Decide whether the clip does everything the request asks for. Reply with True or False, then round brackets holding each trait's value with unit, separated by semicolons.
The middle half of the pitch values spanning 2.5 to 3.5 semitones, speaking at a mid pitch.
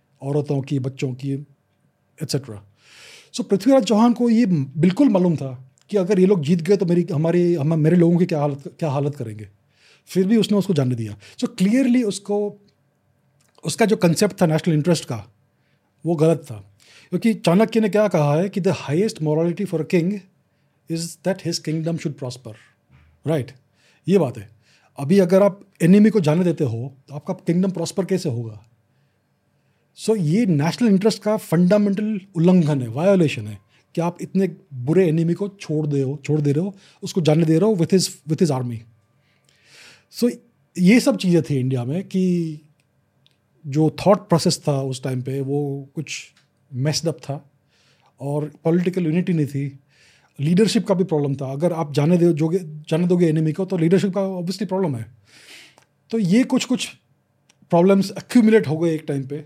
False (5.1 semitones; 165 Hz)